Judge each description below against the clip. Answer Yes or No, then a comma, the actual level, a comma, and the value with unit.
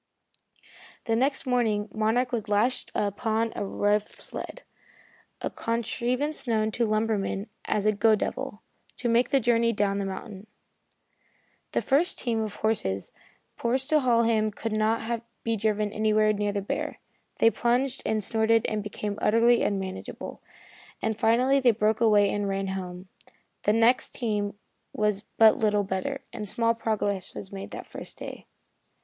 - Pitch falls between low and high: No, high, 220 Hz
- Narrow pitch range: Yes, narrow, 2.2 semitones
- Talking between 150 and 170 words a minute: Yes, average, 155 wpm